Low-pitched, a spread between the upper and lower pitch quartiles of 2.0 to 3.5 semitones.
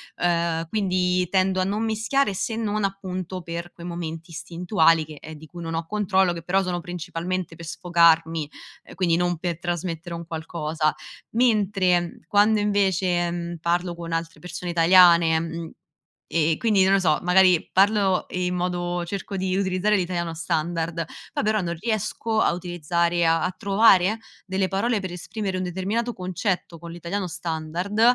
No: medium, 175 Hz; narrow, 2.4 semitones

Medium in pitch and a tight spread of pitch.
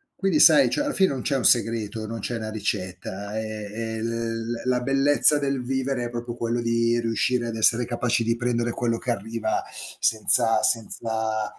No: low, 115 Hz; narrow, 1.9 semitones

